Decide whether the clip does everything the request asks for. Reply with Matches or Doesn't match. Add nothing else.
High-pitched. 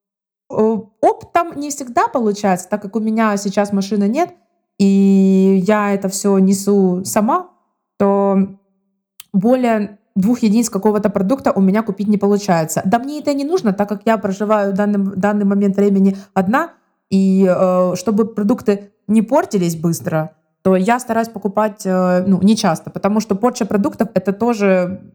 Matches